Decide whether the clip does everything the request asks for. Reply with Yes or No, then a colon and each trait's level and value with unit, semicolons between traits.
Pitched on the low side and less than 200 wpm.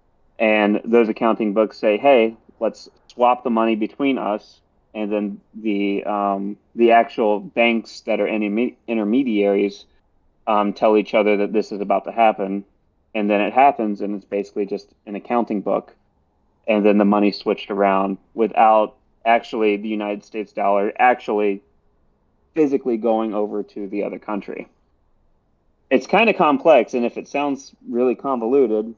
Yes: low, 105 Hz; average, 155 wpm